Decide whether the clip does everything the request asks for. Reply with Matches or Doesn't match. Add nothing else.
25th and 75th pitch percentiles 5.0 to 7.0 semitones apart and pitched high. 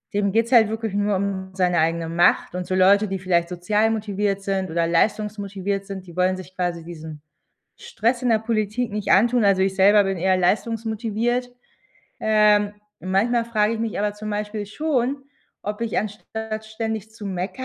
Doesn't match